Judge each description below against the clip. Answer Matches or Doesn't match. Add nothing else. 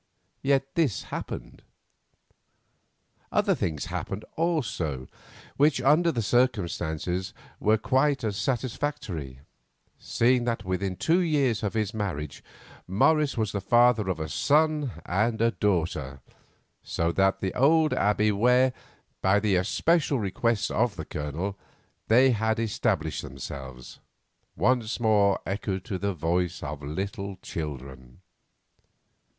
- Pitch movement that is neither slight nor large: Doesn't match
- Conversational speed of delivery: Doesn't match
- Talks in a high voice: Doesn't match